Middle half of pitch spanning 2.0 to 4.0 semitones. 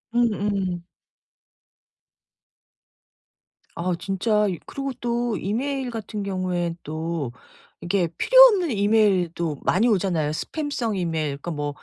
No: wide, 5.4 semitones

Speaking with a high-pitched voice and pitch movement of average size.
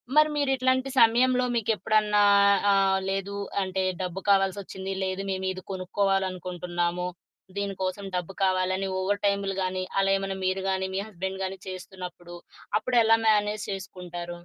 No: high, 195 Hz; narrow, 1.8 semitones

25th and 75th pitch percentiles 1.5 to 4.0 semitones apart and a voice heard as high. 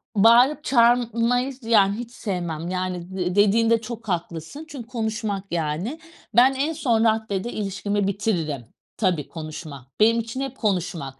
No: average, 4.6 semitones; high, 215 Hz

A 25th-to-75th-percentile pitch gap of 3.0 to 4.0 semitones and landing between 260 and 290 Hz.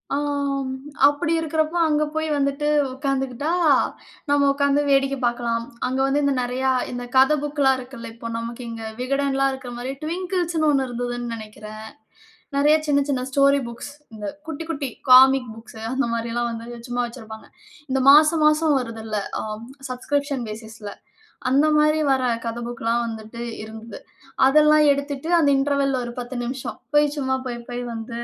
Yes: average, 3.3 semitones; very high, 265 Hz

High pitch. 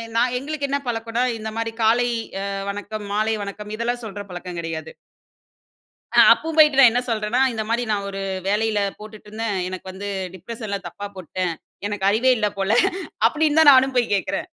Yes: high, 220 Hz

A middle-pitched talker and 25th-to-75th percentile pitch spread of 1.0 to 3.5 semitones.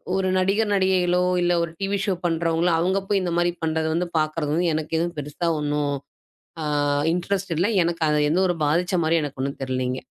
Yes: medium, 170 Hz; average, 3.1 semitones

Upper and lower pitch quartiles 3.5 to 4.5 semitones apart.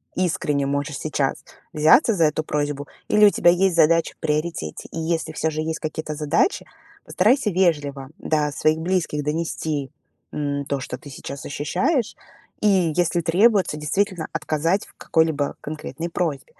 No: average, 3.0 semitones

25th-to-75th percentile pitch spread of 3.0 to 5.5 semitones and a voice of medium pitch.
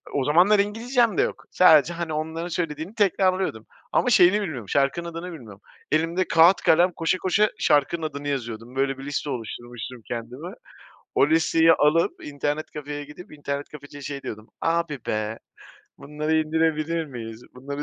Yes: average, 3.7 semitones; medium, 155 Hz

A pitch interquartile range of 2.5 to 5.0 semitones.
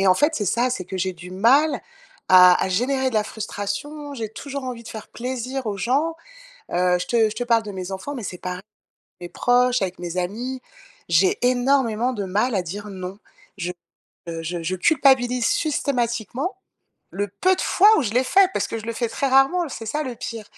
No: wide, 5.6 semitones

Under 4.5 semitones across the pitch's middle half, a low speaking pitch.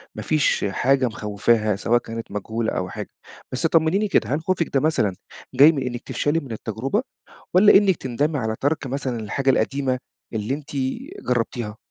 No: average, 5.2 semitones; low, 130 Hz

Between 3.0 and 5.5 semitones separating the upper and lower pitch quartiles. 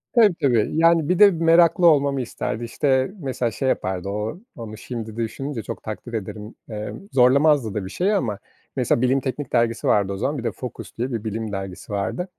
Yes: average, 5.2 semitones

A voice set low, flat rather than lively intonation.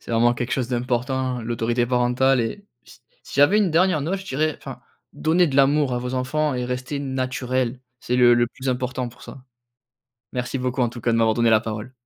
Yes: low, 125 Hz; narrow, 2.1 semitones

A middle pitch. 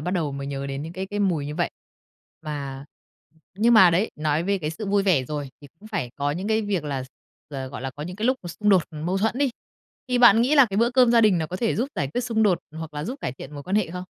Yes: medium, 180 Hz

